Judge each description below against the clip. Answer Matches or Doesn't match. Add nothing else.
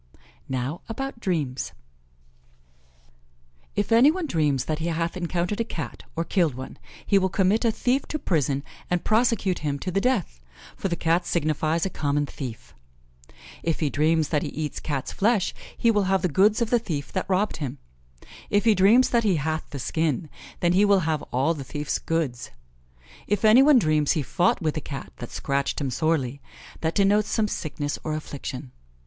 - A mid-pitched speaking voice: Matches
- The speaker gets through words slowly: Doesn't match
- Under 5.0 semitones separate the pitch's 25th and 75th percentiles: Doesn't match